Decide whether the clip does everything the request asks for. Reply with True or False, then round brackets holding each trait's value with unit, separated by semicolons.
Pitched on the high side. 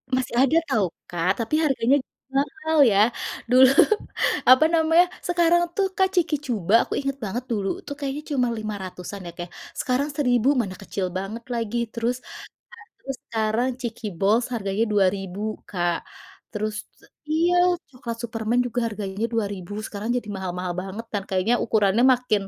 True (230 Hz)